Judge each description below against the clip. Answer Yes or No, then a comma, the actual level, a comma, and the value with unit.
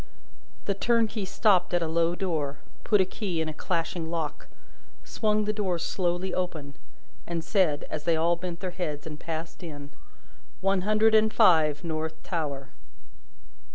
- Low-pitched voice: No, medium, 175 Hz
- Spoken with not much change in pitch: No, average, 3.5 semitones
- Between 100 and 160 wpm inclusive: Yes, average, 155 wpm